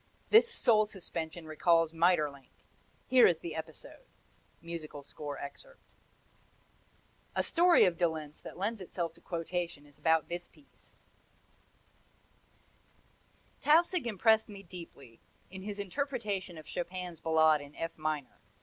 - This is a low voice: No, medium, 170 Hz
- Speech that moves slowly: Yes, slow, 125 wpm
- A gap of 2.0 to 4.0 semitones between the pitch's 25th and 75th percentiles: No, average, 4.6 semitones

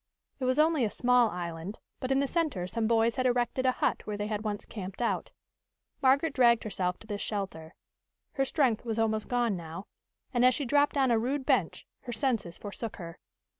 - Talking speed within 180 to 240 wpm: Yes, fast, 205 wpm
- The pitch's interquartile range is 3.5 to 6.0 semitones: Yes, average, 4.1 semitones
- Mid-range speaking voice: No, high, 230 Hz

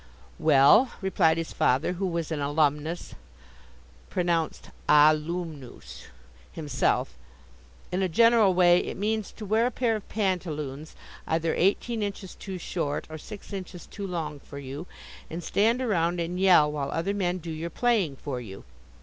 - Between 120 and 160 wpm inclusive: Yes, average, 150 wpm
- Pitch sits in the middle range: Yes, medium, 175 Hz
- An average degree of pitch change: Yes, average, 4.3 semitones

